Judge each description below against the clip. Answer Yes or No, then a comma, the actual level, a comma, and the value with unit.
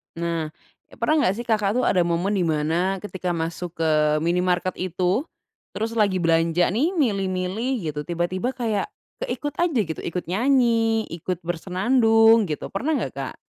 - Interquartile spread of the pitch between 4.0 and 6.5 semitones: Yes, average, 4.9 semitones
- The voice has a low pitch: No, high, 190 Hz